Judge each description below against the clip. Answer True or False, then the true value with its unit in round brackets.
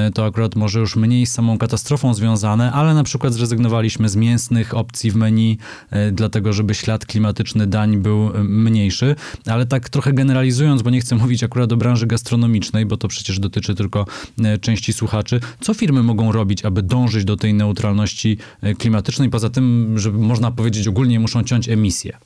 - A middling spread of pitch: False (2.1 semitones)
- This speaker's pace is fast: True (170 wpm)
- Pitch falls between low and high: False (110 Hz)